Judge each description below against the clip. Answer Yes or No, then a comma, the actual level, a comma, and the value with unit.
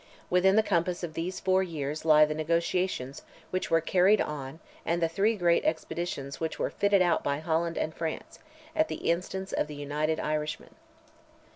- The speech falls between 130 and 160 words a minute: No, average, 175 wpm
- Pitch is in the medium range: Yes, medium, 165 Hz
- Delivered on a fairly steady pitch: No, average, 3.1 semitones